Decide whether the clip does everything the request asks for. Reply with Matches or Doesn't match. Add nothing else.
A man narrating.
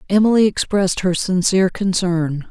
Doesn't match